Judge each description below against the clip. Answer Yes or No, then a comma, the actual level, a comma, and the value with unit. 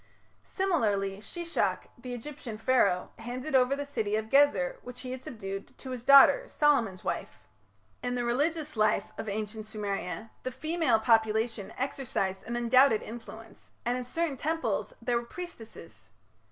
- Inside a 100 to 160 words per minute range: Yes, average, 150 wpm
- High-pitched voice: Yes, high, 245 Hz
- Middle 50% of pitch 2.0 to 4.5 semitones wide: Yes, average, 4.2 semitones